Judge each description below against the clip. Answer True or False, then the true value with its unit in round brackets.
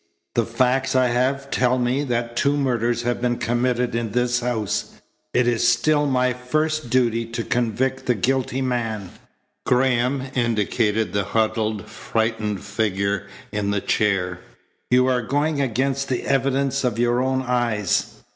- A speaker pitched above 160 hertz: False (120 Hz)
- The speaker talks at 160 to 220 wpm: False (145 wpm)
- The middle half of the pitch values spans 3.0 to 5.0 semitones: False (2.6 semitones)